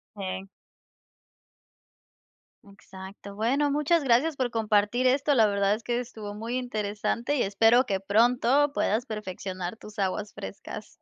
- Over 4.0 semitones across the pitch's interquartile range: No, average, 3.7 semitones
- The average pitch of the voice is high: Yes, high, 220 Hz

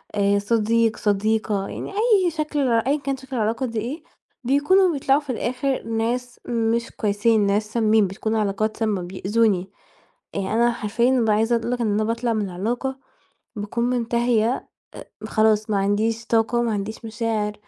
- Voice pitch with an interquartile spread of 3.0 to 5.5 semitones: No, narrow, 2.5 semitones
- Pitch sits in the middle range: No, high, 225 Hz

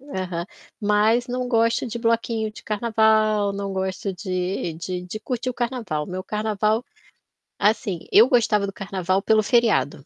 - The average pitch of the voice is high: Yes, high, 210 Hz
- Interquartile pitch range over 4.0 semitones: No, average, 3.4 semitones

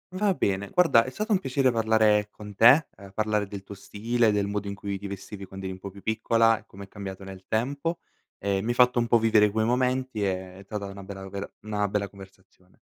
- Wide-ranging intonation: No, average, 2.9 semitones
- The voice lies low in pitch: Yes, low, 105 Hz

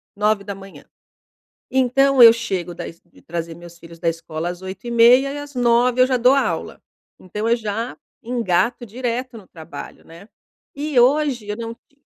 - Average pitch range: No, wide, 5.9 semitones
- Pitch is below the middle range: No, high, 230 Hz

